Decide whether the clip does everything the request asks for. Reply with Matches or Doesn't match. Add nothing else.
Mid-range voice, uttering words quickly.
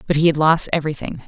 Matches